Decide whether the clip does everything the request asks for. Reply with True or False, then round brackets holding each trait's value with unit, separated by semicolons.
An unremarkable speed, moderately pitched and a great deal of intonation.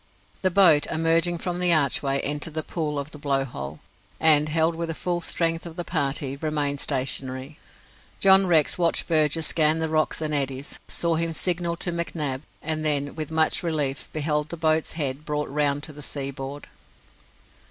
False (180 wpm; 155 Hz; 2.5 semitones)